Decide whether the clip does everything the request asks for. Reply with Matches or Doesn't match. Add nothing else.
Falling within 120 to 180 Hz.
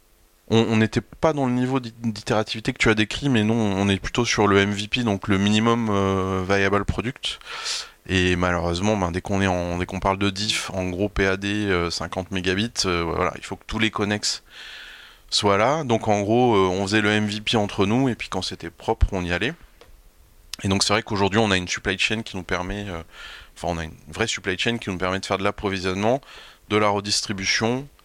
Doesn't match